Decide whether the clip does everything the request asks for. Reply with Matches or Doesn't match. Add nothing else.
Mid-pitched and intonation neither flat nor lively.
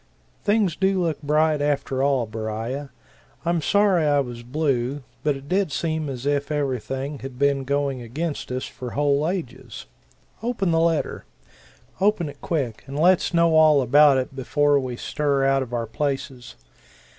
Matches